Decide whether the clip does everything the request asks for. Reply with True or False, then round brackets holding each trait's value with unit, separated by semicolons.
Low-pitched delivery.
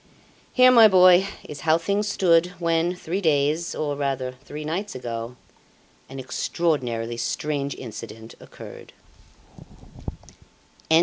False (155 Hz)